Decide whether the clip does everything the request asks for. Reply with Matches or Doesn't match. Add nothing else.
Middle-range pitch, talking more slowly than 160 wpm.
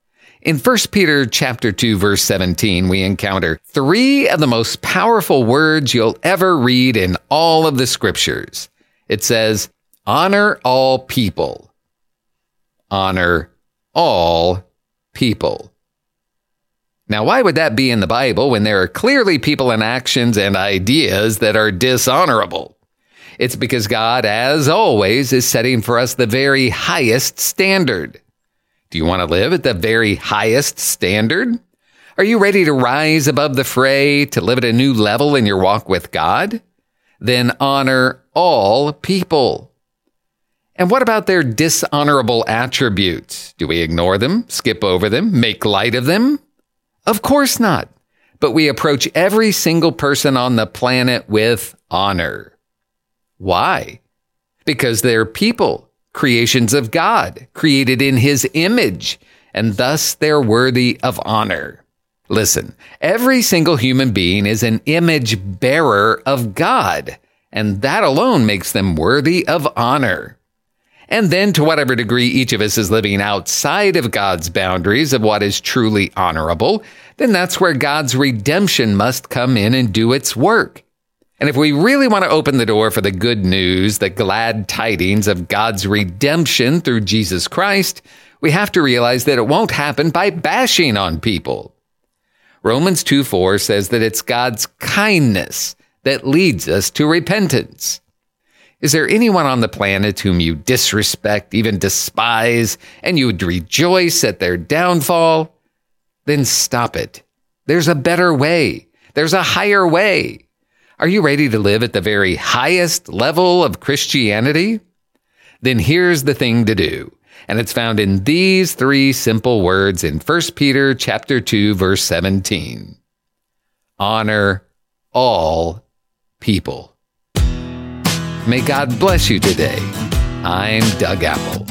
Doesn't match